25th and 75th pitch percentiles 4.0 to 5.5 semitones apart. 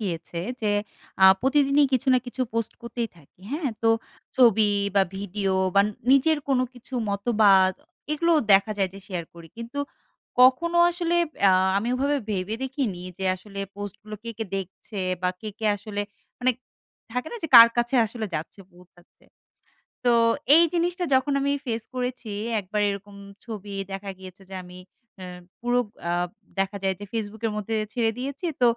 Yes: average, 4.5 semitones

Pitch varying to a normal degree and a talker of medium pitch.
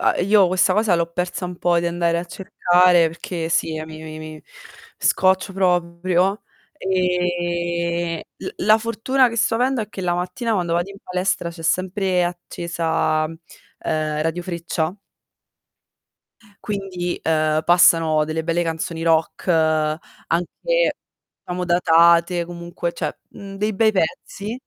No: narrow, 2.1 semitones; medium, 175 Hz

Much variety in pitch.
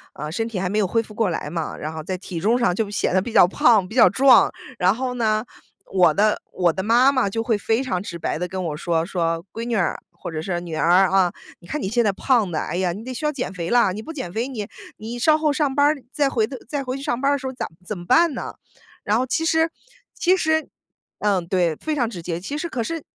Yes: wide, 6.2 semitones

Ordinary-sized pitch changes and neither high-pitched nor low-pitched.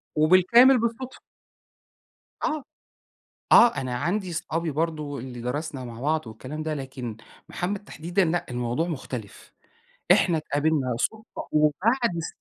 No: wide, 5.8 semitones; medium, 155 Hz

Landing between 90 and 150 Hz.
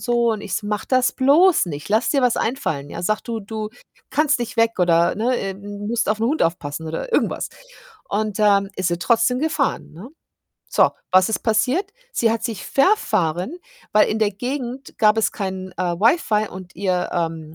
No: high, 215 Hz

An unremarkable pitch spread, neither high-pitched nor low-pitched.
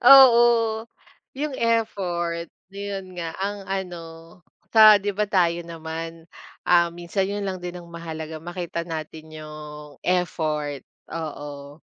Yes: average, 3.8 semitones; medium, 175 Hz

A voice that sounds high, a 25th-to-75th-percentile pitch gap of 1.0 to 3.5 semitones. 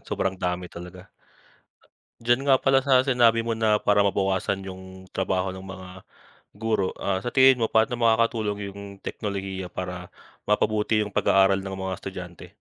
No: low, 100 Hz; average, 3.2 semitones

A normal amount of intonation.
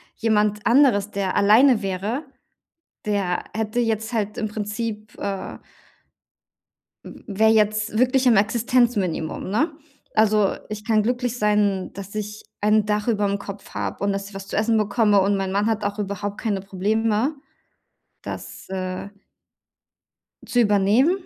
No: narrow, 1.9 semitones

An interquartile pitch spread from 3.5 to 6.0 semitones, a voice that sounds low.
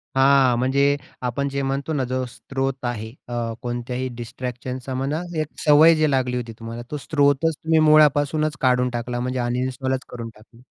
No: narrow, 2.4 semitones; low, 130 Hz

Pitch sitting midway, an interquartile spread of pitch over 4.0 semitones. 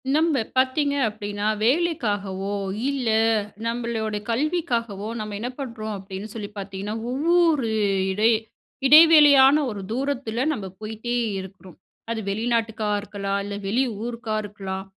No: high, 225 Hz; average, 4.6 semitones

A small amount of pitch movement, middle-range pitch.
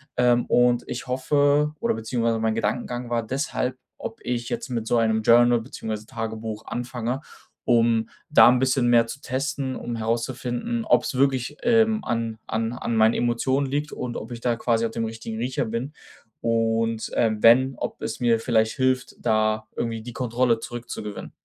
No: narrow, 2.2 semitones; low, 120 Hz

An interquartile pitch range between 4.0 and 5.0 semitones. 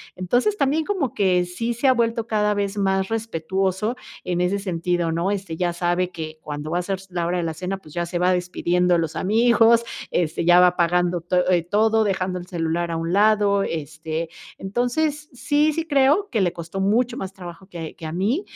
Yes: average, 4.3 semitones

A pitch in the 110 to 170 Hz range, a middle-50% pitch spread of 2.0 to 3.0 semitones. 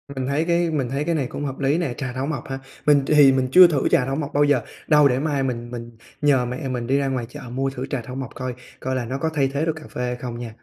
Yes: low, 135 Hz; narrow, 2.6 semitones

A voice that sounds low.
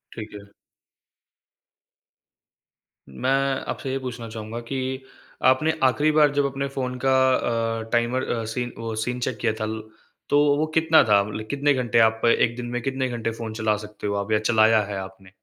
Yes: low, 120 Hz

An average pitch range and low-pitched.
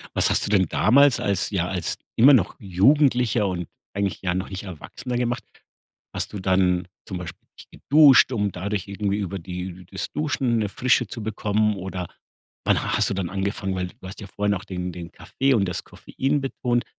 Yes: average, 4.4 semitones; low, 100 Hz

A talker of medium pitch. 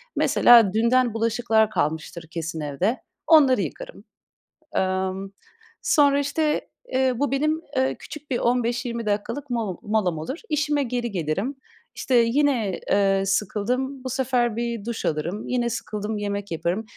No: high, 235 Hz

